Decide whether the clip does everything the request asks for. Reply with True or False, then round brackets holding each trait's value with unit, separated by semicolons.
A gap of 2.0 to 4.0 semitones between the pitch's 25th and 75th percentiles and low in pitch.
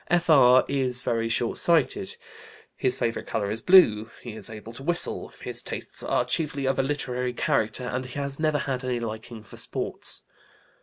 True (3.4 semitones; 125 Hz)